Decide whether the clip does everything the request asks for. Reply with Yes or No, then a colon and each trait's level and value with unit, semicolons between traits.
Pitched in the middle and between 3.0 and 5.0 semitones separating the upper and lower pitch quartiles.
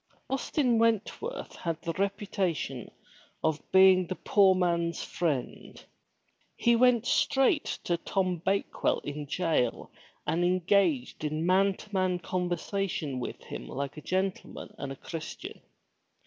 Yes: medium, 180 Hz; average, 3.7 semitones